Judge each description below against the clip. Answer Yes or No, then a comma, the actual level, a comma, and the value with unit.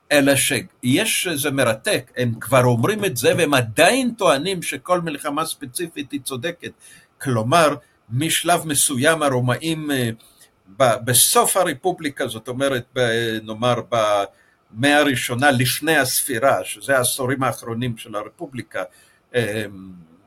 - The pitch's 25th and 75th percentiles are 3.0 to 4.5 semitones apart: Yes, average, 3.8 semitones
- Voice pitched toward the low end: Yes, low, 130 Hz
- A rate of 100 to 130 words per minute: Yes, average, 105 wpm